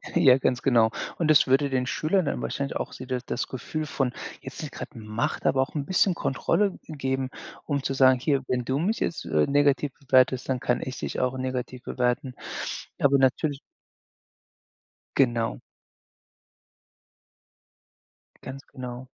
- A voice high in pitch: No, low, 130 Hz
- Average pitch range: No, narrow, 2.0 semitones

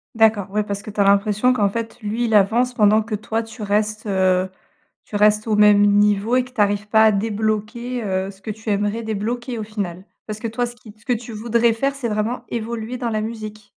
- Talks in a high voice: Yes, high, 215 Hz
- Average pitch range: No, narrow, 2.0 semitones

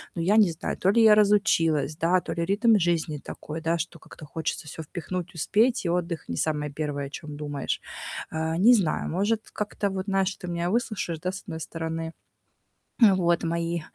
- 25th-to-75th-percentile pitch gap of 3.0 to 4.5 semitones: Yes, average, 3.4 semitones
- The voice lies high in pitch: No, medium, 170 Hz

